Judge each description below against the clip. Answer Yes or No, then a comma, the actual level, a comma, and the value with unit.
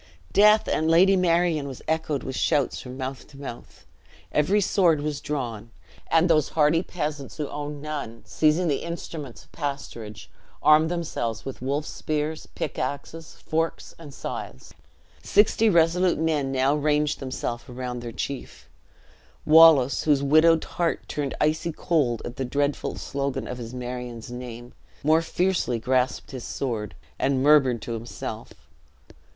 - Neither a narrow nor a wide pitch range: Yes, average, 4.0 semitones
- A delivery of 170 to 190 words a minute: No, average, 145 wpm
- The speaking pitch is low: No, medium, 145 Hz